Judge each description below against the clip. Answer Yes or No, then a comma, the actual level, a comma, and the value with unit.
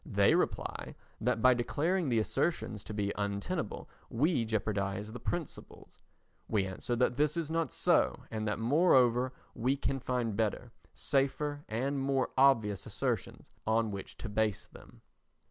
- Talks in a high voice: No, low, 120 Hz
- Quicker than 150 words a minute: No, average, 145 wpm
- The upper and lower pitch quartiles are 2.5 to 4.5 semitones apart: Yes, average, 4.2 semitones